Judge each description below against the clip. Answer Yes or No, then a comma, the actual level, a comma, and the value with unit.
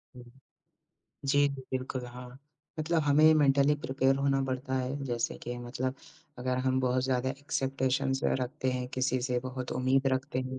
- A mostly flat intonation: Yes, narrow, 1.2 semitones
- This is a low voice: Yes, low, 130 Hz